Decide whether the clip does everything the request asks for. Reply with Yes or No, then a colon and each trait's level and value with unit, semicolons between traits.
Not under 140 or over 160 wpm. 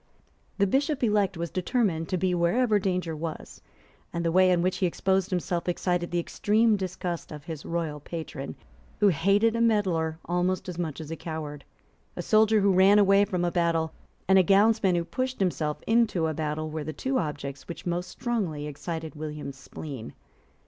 No: average, 185 wpm